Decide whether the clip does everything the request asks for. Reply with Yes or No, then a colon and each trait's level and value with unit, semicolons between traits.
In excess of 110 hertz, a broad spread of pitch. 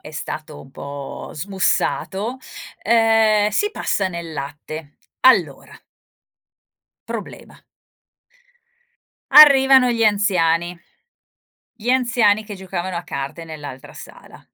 Yes: high, 190 Hz; wide, 6.2 semitones